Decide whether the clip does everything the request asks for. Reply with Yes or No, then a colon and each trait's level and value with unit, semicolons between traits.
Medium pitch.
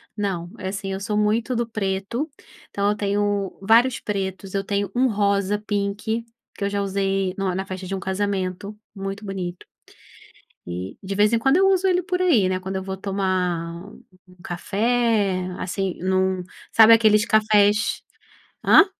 No: high, 200 Hz